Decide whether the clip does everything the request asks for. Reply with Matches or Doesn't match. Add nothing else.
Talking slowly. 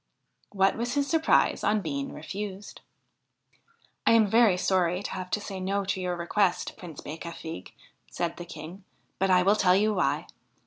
Doesn't match